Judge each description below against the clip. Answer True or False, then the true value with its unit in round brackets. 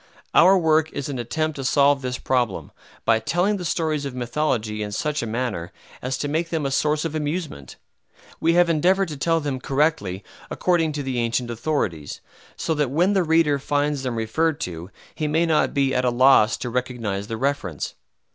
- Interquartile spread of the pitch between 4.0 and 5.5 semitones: True (4.8 semitones)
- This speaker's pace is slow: False (195 wpm)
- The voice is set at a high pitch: False (140 Hz)